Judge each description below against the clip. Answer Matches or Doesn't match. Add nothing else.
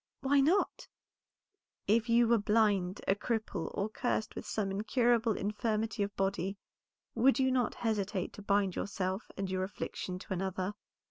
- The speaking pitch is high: Matches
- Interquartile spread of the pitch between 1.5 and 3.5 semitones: Matches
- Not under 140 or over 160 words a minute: Matches